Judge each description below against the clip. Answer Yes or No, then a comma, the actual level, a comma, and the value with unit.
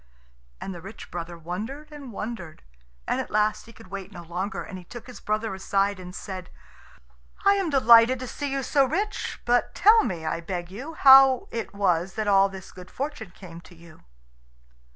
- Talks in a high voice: Yes, high, 200 Hz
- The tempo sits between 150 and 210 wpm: Yes, average, 195 wpm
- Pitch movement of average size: No, wide, 6.1 semitones